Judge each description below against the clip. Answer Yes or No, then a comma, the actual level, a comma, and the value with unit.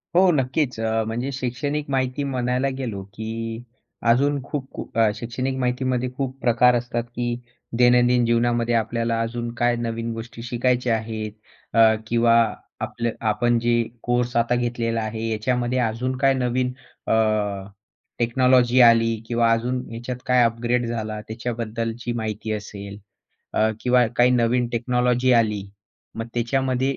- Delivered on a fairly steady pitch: Yes, narrow, 1.6 semitones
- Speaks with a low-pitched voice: Yes, low, 120 Hz